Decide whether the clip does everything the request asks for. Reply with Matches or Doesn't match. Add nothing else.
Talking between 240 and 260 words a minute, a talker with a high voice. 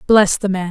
Matches